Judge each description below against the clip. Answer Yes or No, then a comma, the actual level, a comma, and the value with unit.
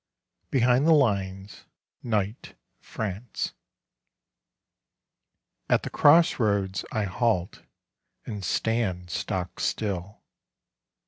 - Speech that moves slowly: Yes, slow, 80 wpm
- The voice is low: Yes, low, 105 Hz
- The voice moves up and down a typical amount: Yes, average, 4.0 semitones